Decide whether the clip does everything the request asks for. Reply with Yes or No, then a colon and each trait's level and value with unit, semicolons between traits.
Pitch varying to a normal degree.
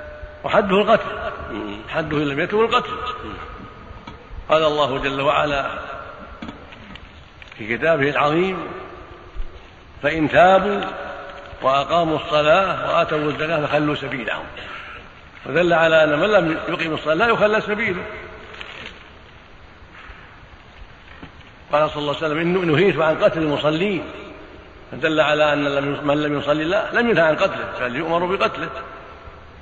Yes: average, 3.3 semitones